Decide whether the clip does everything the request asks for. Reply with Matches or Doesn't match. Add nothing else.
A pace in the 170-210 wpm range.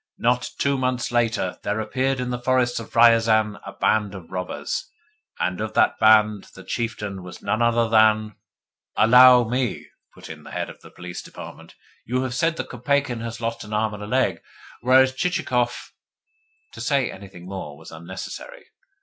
Matches